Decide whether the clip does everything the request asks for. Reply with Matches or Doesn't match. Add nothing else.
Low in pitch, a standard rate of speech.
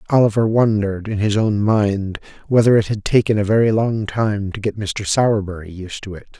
Matches